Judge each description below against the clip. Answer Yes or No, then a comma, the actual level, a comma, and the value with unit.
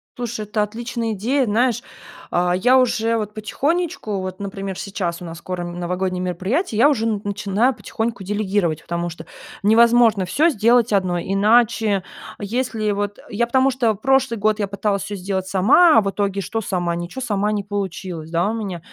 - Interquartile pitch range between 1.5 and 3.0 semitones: No, average, 3.7 semitones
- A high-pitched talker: Yes, high, 210 Hz